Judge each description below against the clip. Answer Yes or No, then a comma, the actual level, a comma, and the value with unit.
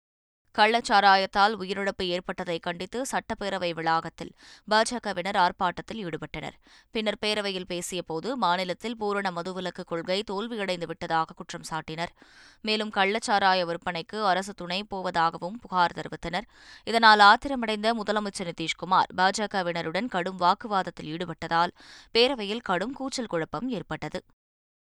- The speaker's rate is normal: Yes, average, 100 wpm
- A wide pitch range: No, average, 3.4 semitones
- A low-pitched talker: No, medium, 185 Hz